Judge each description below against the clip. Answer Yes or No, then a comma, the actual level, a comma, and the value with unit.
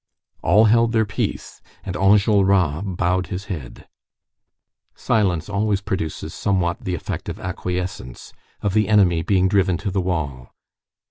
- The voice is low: Yes, very low, 95 Hz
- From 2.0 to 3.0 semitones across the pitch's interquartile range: Yes, narrow, 2.5 semitones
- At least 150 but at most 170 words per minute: No, slow, 135 wpm